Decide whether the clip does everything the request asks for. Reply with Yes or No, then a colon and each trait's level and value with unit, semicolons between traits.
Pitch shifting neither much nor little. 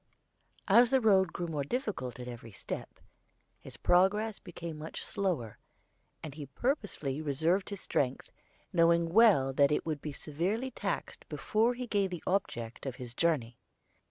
No: wide, 6.6 semitones